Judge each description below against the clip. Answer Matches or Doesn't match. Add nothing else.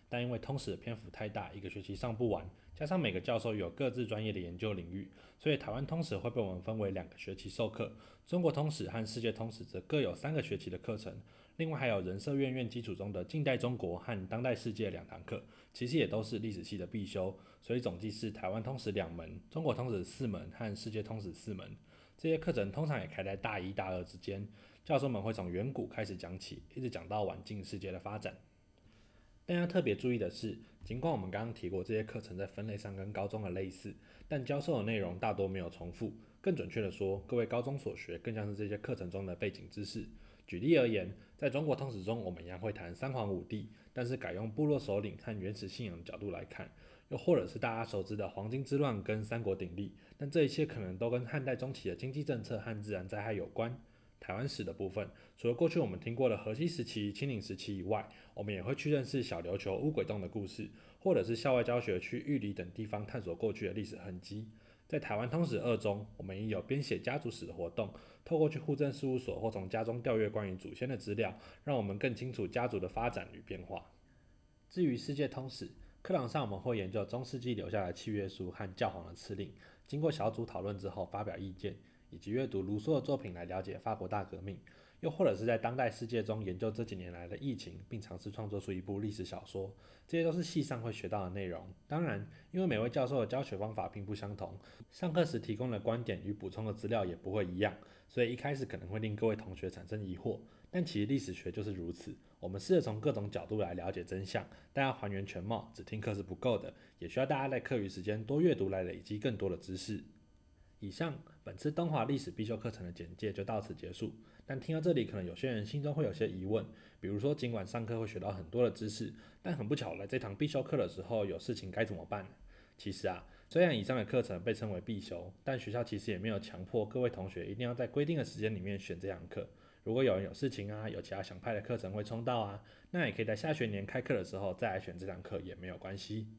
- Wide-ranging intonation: Doesn't match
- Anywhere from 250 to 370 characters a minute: Matches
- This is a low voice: Matches